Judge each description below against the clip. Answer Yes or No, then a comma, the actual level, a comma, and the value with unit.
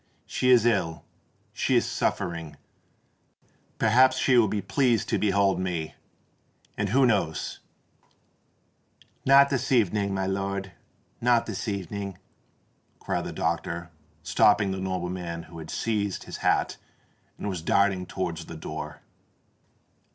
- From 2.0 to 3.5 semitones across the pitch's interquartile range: No, average, 4.2 semitones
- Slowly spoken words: Yes, slow, 115 wpm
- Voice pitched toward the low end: Yes, very low, 95 Hz